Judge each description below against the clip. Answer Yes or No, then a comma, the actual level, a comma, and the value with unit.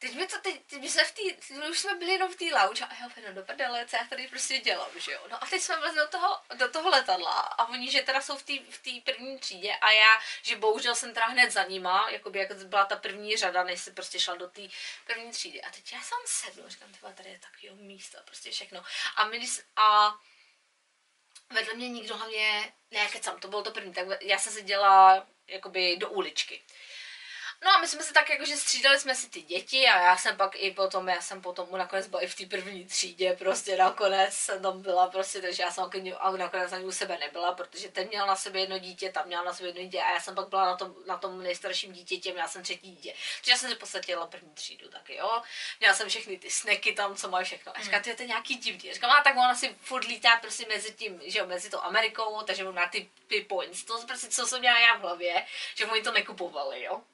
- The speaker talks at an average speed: No, fast, 235 wpm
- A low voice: No, high, 205 Hz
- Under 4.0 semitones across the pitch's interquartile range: No, average, 4.9 semitones